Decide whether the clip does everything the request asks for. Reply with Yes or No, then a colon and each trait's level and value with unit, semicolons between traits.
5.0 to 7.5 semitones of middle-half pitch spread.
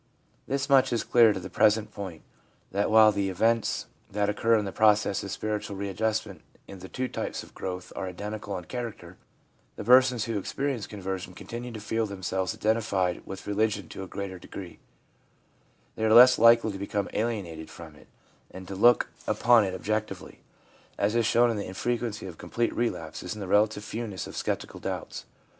No: average, 3.2 semitones